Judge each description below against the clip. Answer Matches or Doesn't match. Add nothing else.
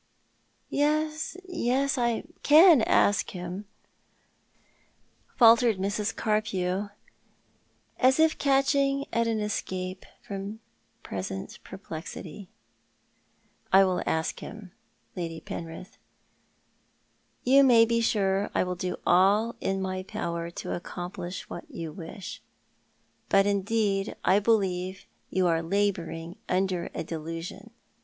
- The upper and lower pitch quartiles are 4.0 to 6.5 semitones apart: Matches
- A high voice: Matches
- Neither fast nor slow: Doesn't match